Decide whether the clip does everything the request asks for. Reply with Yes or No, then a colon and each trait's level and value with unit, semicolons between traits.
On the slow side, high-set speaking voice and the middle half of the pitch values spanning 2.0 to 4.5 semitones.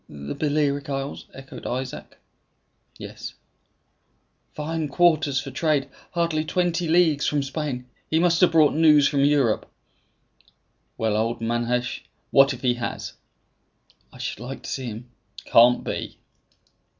No: slow, 130 wpm; medium, 140 Hz; average, 4.1 semitones